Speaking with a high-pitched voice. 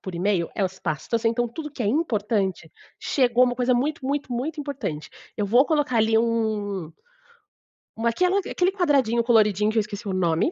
Yes: high, 230 Hz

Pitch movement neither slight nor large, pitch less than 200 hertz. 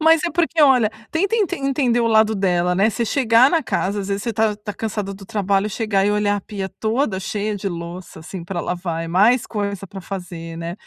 No: average, 3.5 semitones; high, 205 Hz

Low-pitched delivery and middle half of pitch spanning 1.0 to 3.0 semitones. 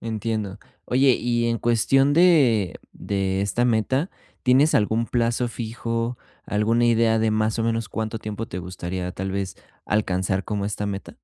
Yes: low, 110 Hz; average, 2.7 semitones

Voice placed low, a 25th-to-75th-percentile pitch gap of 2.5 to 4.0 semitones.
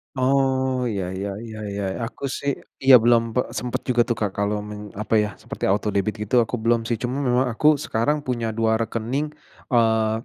Yes: low, 115 Hz; average, 2.9 semitones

